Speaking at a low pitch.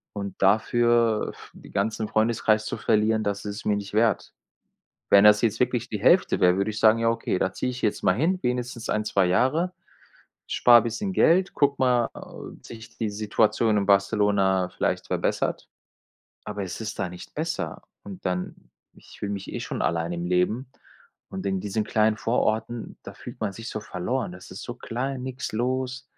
Yes: low, 110 Hz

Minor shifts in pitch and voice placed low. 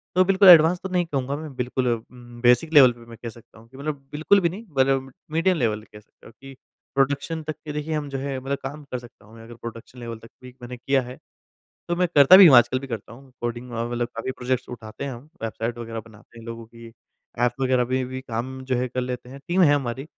No: average, 3.5 semitones; low, 130 Hz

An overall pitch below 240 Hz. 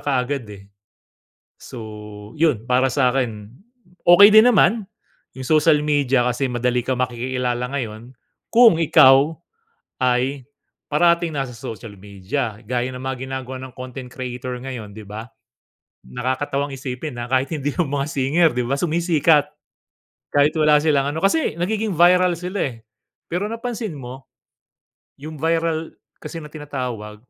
Yes: low, 135 Hz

